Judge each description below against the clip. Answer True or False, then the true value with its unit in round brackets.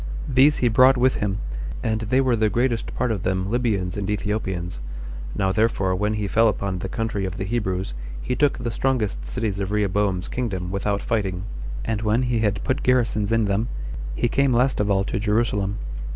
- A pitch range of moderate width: True (3.4 semitones)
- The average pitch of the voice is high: False (105 Hz)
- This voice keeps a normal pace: True (195 wpm)